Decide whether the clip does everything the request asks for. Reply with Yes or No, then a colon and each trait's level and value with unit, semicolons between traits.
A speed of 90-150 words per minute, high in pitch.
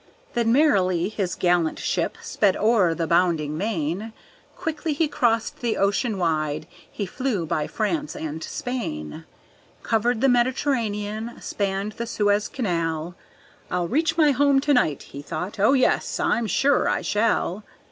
Yes: average, 145 wpm; high, 210 Hz